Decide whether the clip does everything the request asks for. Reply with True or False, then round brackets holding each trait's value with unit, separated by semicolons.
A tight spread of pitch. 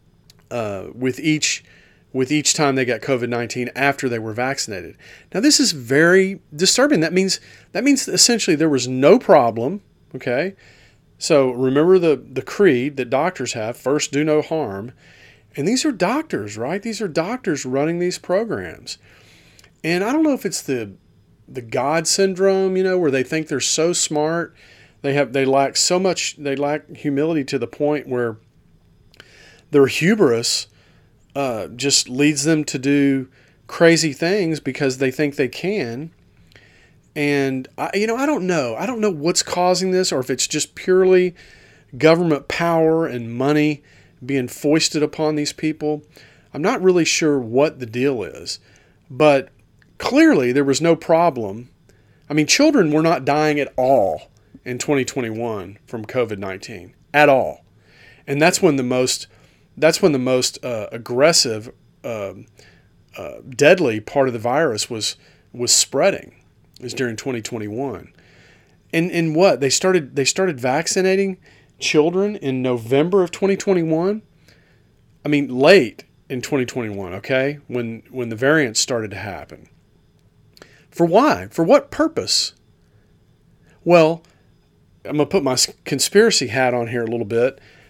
False (4.9 semitones)